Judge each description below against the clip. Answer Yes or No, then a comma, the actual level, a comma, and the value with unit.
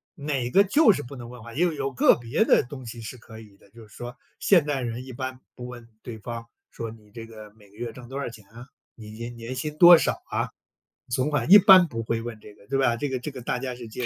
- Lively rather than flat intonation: No, average, 3.1 semitones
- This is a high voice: No, low, 120 Hz